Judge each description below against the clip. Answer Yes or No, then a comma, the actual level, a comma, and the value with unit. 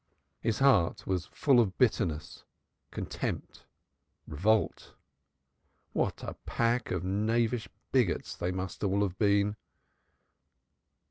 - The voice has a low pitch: Yes, low, 100 Hz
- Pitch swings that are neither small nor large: Yes, average, 3.8 semitones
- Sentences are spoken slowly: Yes, slow, 105 wpm